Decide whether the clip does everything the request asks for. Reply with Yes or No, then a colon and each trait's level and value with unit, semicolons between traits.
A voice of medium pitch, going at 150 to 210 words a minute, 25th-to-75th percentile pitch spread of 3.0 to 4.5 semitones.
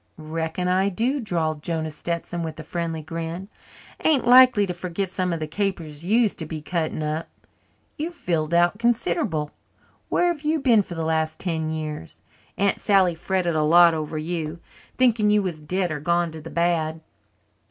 Yes: medium, 170 Hz; average, 180 wpm; average, 3.8 semitones